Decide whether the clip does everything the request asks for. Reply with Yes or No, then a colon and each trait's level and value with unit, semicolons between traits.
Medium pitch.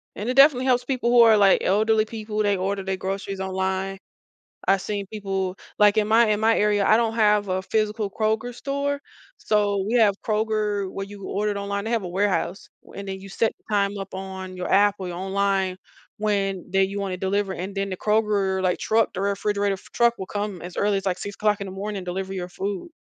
No: high, 200 Hz